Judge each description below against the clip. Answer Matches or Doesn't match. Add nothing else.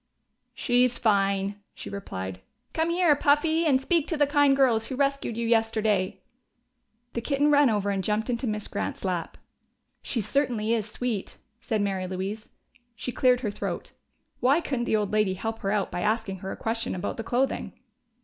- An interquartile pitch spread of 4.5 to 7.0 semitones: Matches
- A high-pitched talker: Matches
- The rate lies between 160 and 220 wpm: Matches